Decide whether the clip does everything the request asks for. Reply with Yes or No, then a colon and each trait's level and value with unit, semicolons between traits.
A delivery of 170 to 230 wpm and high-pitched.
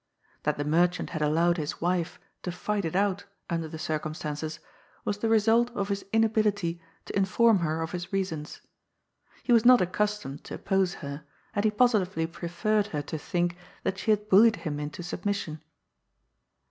No: average, 175 wpm; medium, 180 Hz